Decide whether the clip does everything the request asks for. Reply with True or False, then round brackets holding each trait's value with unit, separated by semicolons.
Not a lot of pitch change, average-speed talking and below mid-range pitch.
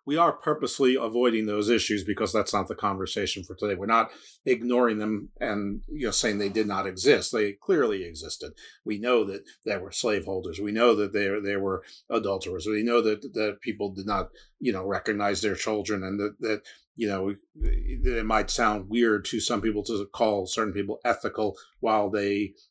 True (1.7 semitones; 190 wpm; 105 Hz)